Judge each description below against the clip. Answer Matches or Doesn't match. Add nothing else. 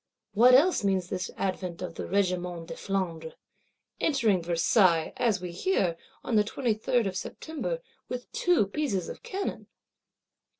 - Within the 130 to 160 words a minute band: Matches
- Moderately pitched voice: Doesn't match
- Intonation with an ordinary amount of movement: Doesn't match